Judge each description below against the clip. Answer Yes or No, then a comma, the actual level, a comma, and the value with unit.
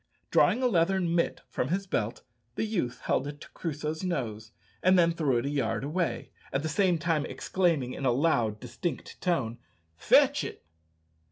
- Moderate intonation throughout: No, wide, 5.8 semitones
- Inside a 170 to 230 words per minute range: Yes, average, 175 wpm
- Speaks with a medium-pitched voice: Yes, medium, 155 Hz